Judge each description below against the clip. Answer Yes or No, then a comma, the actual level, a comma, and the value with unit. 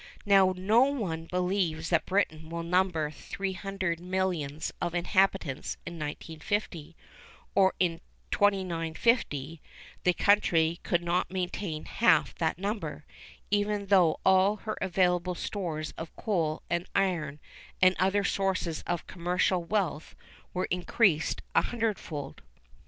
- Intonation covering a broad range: No, average, 3.0 semitones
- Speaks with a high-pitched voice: No, medium, 180 Hz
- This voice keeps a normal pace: No, slow, 120 wpm